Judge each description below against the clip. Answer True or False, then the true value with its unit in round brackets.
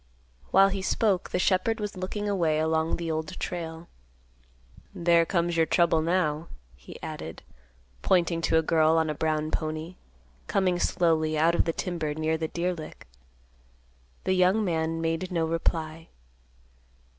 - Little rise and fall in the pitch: True (2.2 semitones)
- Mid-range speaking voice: True (165 Hz)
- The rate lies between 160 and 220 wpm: False (150 wpm)